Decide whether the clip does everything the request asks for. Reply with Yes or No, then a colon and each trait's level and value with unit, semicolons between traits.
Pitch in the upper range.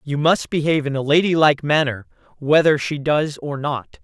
No: medium, 145 Hz